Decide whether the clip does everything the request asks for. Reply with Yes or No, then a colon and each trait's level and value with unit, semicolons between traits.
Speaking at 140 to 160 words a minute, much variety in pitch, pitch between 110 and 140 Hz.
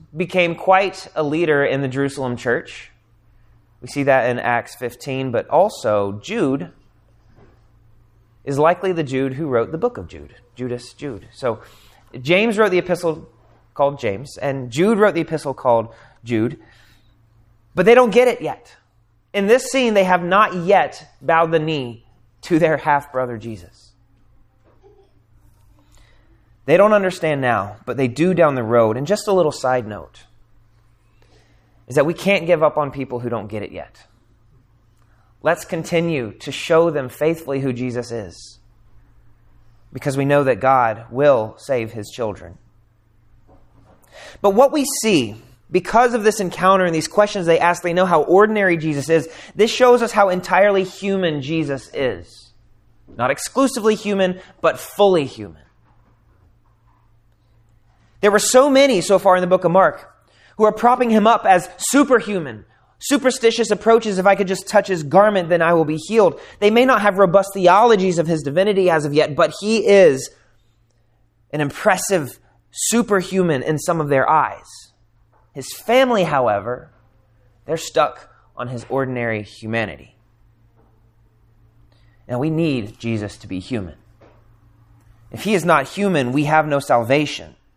Yes: average, 155 wpm; wide, 8.2 semitones; low, 135 Hz